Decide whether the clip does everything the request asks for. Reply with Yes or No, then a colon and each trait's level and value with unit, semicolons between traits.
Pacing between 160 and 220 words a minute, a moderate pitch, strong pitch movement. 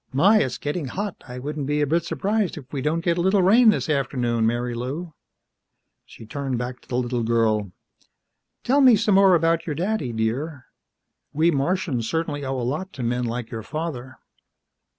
Yes: average, 185 wpm; medium, 145 Hz; wide, 5.8 semitones